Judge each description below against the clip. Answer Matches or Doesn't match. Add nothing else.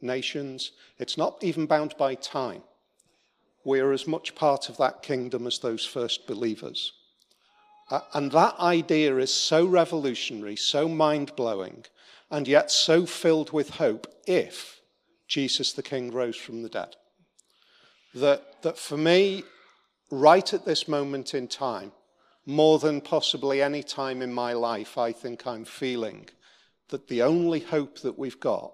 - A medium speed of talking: Matches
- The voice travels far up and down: Doesn't match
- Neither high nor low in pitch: Matches